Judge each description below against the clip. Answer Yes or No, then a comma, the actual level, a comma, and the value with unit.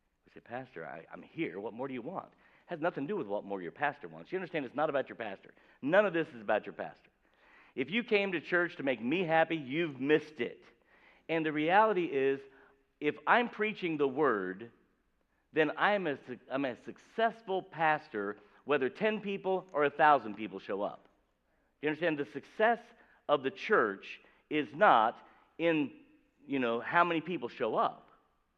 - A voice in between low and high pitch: Yes, medium, 155 Hz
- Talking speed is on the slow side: No, average, 185 wpm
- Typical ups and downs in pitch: No, wide, 6.3 semitones